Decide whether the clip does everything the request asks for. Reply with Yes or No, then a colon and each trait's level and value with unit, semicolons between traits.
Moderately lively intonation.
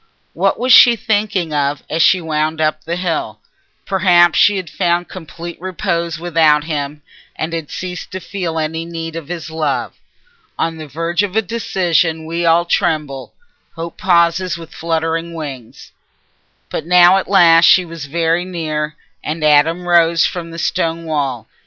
No: narrow, 1.9 semitones